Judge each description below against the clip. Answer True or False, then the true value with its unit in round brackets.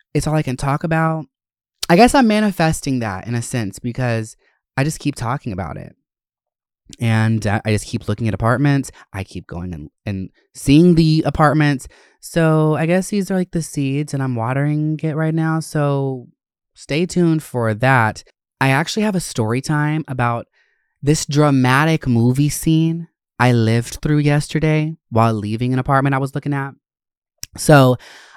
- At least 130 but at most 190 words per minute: True (165 wpm)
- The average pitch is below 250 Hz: True (140 Hz)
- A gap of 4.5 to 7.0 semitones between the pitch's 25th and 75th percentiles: True (4.8 semitones)